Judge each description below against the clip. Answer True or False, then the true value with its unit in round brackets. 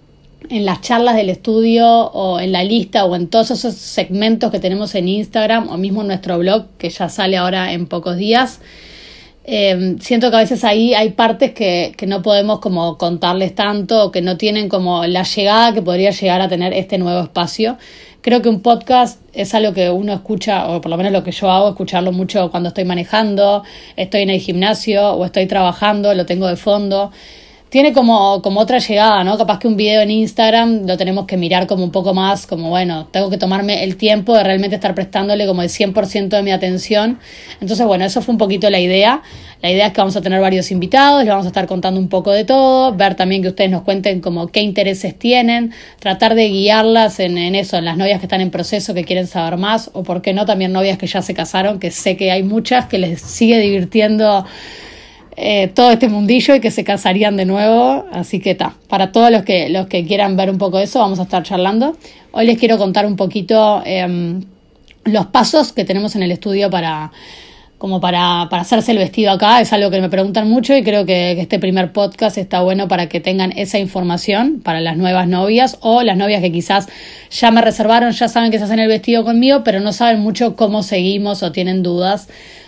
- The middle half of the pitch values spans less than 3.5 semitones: True (2.9 semitones)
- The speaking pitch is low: False (200 Hz)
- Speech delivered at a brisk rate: True (220 wpm)